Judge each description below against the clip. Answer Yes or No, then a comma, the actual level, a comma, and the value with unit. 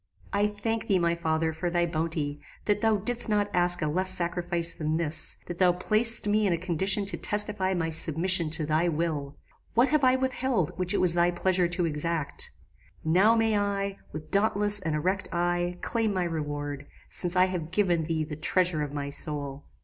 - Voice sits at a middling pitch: Yes, medium, 175 Hz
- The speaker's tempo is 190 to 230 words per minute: Yes, average, 195 wpm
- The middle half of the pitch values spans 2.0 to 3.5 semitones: No, average, 4.1 semitones